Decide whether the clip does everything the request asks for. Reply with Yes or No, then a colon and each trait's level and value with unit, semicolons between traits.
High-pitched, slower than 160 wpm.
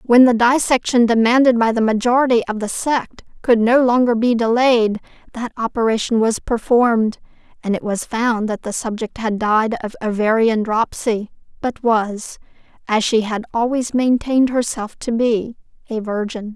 Yes: high, 230 Hz; average, 150 wpm